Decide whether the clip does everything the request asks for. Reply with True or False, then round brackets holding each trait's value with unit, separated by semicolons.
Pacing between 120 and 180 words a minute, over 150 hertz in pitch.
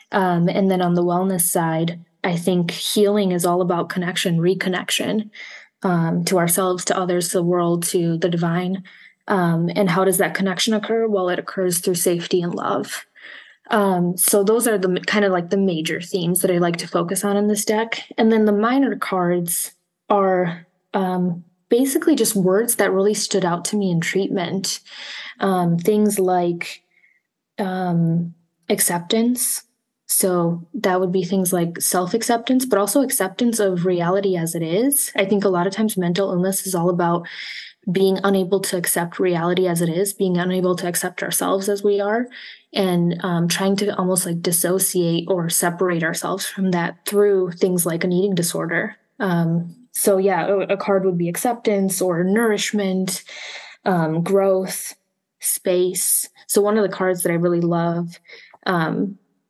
True (170 wpm; 185 Hz)